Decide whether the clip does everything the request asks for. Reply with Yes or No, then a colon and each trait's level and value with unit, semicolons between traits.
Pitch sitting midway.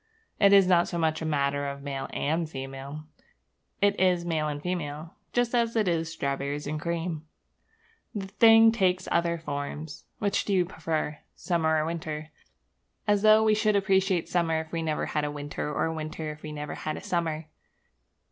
Yes: medium, 160 Hz